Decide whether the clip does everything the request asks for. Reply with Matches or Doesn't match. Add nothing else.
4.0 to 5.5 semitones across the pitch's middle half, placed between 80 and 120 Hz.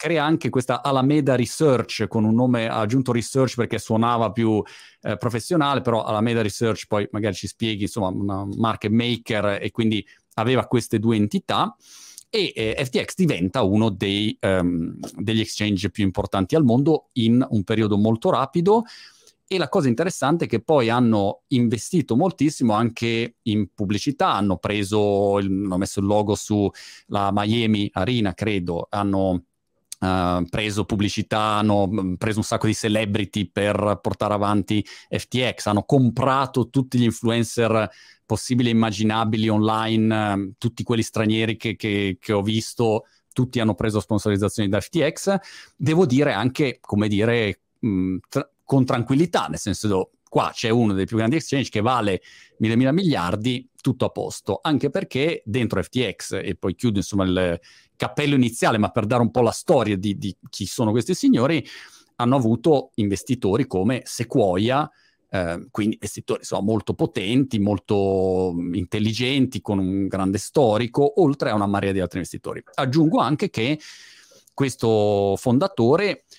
Doesn't match